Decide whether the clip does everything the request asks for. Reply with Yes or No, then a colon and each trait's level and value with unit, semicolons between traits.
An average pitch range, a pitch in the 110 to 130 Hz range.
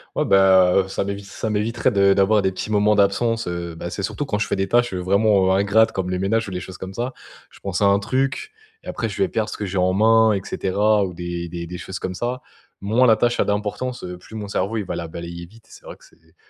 No: average, 3.1 semitones; low, 100 Hz